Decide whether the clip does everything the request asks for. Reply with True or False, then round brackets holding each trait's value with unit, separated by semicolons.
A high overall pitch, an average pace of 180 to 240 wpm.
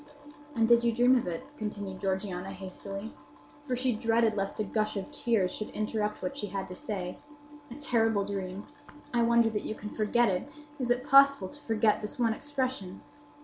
True (215 Hz; 190 wpm)